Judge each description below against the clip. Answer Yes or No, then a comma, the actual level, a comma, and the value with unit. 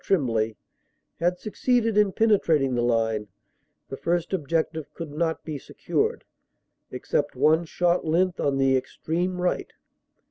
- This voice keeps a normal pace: No, slow, 130 wpm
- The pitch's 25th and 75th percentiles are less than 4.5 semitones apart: No, average, 5.0 semitones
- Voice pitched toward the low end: No, medium, 160 Hz